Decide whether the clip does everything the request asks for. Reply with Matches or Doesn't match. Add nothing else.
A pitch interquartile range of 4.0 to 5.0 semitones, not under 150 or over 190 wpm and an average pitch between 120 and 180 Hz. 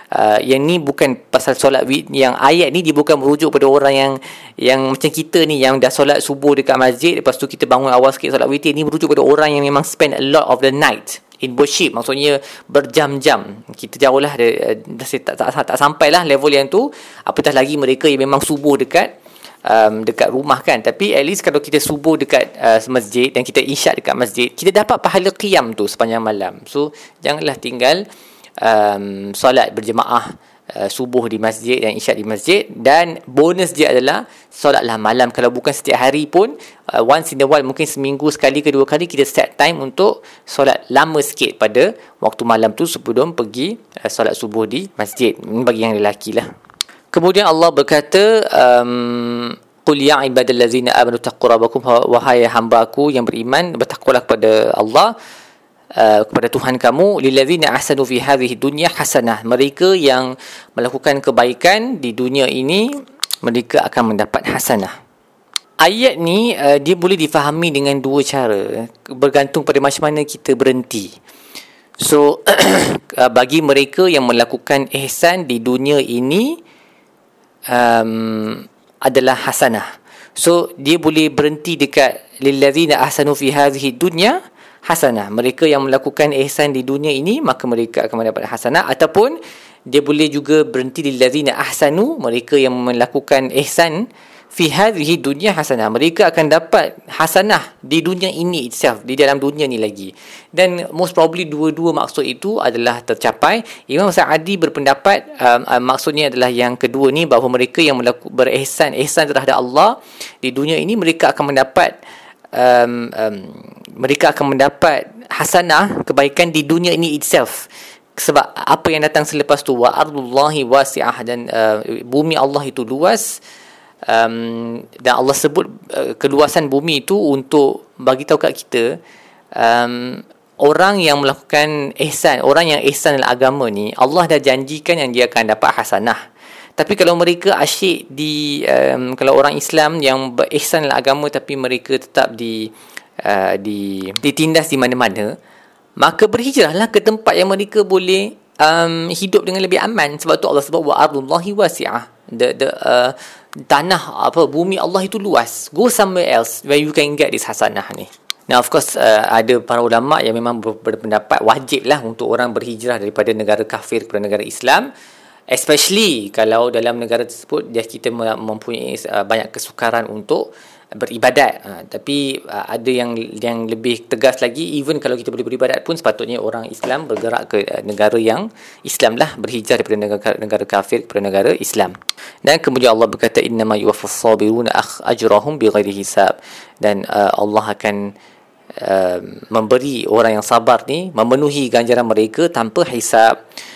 Matches